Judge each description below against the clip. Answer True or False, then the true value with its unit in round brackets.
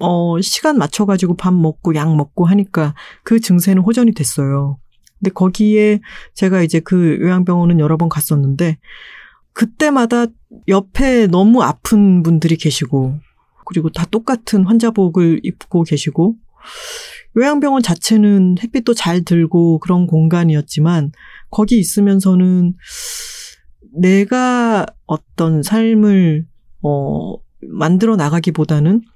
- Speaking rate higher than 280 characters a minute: False (255 characters per minute)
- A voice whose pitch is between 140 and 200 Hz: True (185 Hz)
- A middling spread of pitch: True (4.9 semitones)